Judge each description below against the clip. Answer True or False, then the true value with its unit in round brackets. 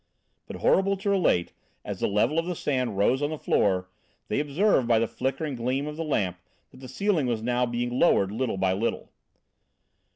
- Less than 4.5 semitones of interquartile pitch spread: False (5.3 semitones)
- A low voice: True (130 Hz)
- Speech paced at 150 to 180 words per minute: False (195 wpm)